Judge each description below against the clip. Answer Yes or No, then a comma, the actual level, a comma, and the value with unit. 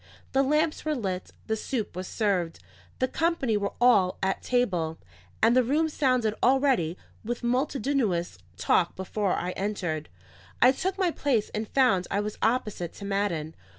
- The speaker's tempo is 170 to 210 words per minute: No, average, 155 wpm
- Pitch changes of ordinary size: No, wide, 5.9 semitones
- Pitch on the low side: No, high, 220 Hz